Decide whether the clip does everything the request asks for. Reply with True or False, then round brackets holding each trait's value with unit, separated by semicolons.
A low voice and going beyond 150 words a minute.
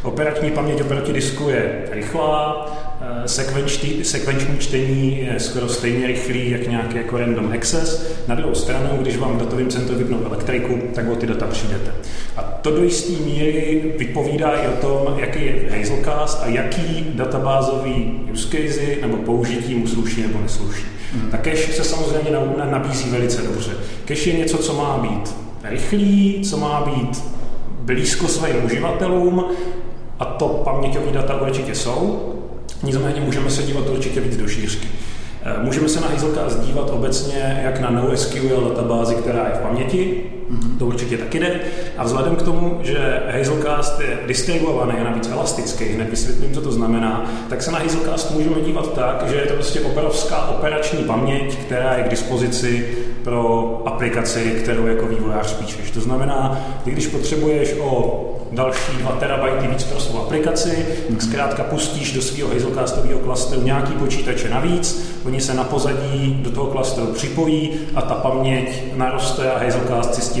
True (130 Hz; 160 wpm)